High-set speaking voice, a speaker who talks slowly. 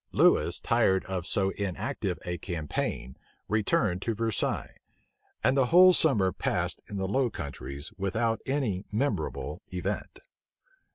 No: low, 100 Hz; slow, 125 wpm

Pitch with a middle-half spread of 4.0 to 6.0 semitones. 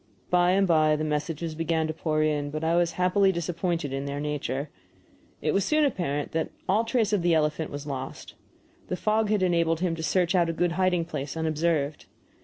No: average, 2.9 semitones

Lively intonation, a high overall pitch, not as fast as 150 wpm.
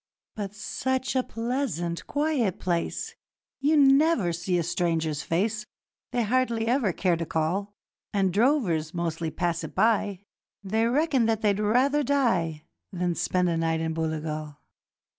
Yes: wide, 6.6 semitones; high, 200 Hz; average, 140 wpm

